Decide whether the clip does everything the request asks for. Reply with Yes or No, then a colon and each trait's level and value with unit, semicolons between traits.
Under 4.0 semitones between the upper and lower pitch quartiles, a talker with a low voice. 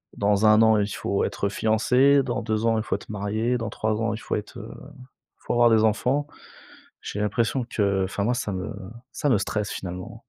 Yes: narrow, 2.4 semitones; low, 110 Hz